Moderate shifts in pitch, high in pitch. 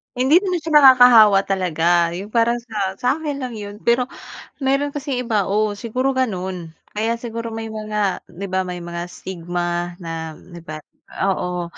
No: wide, 5.8 semitones; high, 210 Hz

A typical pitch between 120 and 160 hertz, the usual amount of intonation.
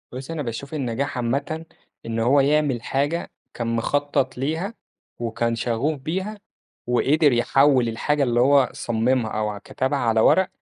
Yes: low, 135 Hz; average, 3.8 semitones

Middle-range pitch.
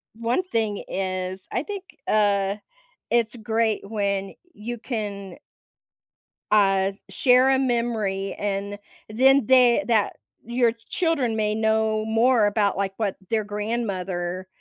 No: high, 215 Hz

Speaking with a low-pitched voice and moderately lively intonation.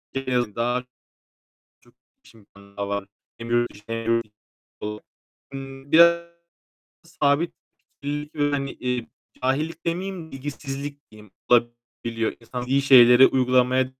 Yes: low, 125 Hz; average, 3.6 semitones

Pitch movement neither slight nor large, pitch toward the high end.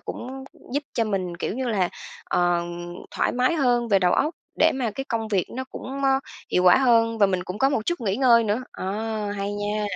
Yes: average, 4.9 semitones; high, 225 Hz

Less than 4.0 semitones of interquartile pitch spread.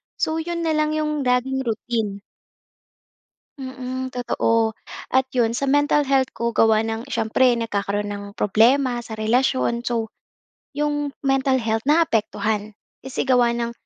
Yes: average, 3.4 semitones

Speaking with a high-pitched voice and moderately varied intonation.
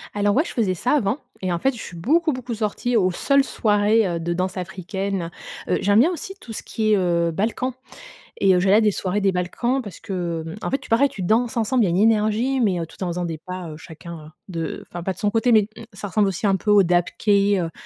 Yes: high, 200 Hz; average, 4.0 semitones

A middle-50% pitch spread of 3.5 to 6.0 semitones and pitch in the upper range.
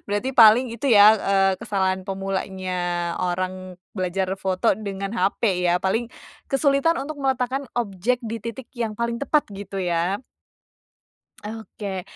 Yes: average, 3.9 semitones; high, 200 Hz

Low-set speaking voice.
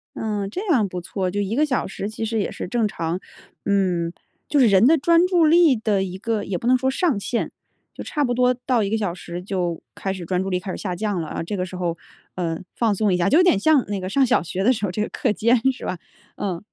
No: high, 205 Hz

